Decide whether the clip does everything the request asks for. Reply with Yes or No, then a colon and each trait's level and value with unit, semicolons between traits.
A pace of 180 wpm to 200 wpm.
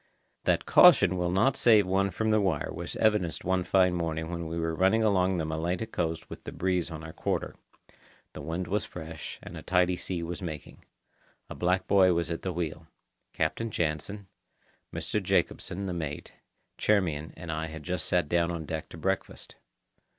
Yes: average, 185 wpm